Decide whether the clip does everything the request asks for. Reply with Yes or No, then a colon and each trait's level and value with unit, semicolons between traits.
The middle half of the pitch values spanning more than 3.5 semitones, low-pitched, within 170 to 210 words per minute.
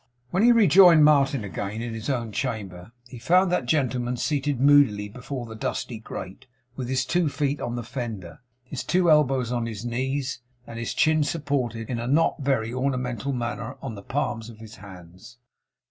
Yes: average, 3.9 semitones; low, 125 Hz; average, 180 wpm